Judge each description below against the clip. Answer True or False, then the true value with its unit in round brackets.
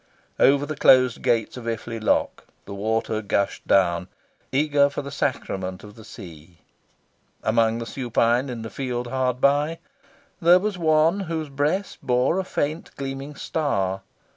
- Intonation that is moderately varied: True (4.7 semitones)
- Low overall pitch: True (130 Hz)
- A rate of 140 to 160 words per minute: True (150 wpm)